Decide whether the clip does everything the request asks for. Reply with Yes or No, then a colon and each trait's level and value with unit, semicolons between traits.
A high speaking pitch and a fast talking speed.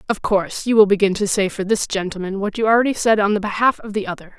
Yes: high, 205 Hz; fast, 275 wpm